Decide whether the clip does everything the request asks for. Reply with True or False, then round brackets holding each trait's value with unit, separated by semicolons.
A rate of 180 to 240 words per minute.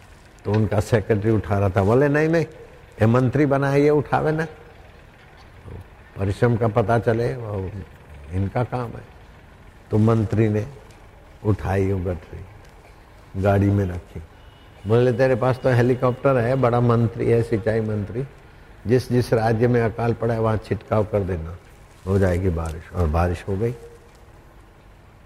False (145 wpm)